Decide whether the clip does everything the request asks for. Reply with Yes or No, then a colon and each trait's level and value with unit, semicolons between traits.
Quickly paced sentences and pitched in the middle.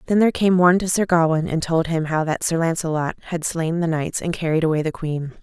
Yes: fast, 255 wpm; medium, 165 Hz